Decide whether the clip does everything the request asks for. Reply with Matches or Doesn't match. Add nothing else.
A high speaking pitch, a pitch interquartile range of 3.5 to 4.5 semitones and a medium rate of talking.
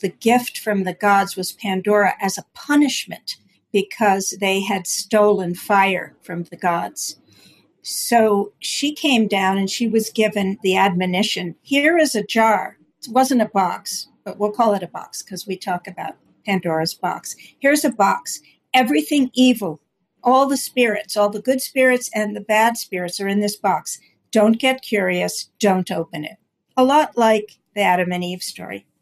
Matches